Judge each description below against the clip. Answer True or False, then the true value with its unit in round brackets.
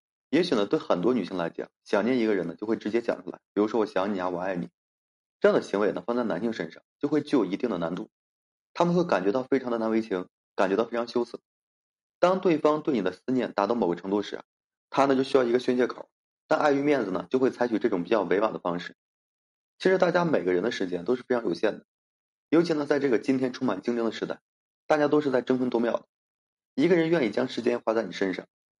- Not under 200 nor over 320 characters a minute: False (360 characters per minute)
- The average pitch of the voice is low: True (125 Hz)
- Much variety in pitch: False (4.7 semitones)